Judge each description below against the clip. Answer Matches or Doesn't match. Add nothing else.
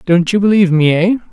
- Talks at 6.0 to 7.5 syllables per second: Matches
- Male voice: Matches